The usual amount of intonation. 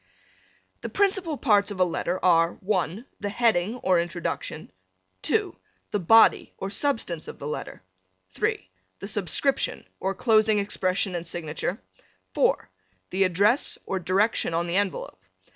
Yes: average, 3.8 semitones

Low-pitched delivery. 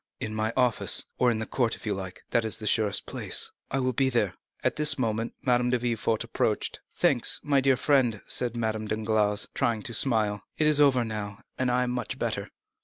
Yes: low, 115 Hz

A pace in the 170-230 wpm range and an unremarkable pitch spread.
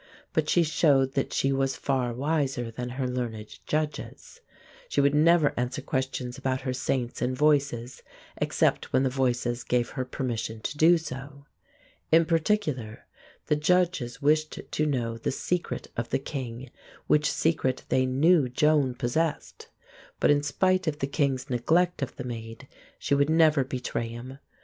No: average, 160 wpm; average, 3.4 semitones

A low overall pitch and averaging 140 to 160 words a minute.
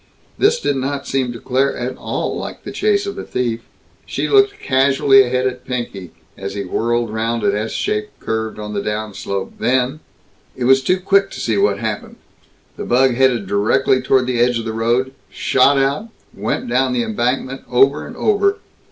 No: low, 125 Hz; average, 185 wpm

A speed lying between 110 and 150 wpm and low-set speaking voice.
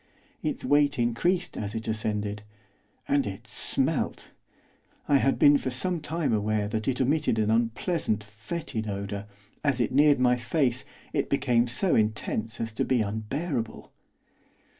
Yes: average, 145 wpm; low, 120 Hz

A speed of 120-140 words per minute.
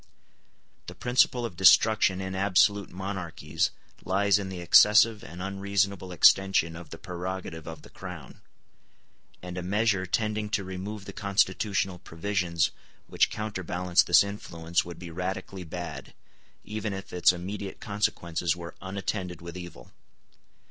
Yes: slow, 135 wpm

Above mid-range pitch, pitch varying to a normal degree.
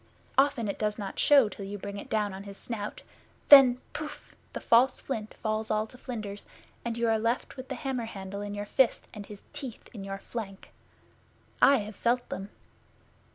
Yes: high, 220 Hz; average, 3.5 semitones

